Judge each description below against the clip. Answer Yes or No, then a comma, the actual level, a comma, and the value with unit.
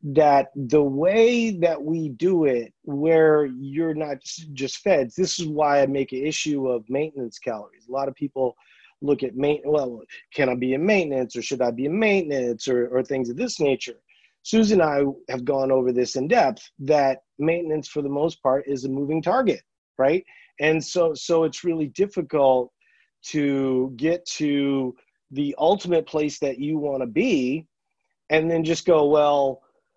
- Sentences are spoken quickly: No, average, 180 wpm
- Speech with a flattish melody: No, average, 3.3 semitones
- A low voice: No, medium, 145 Hz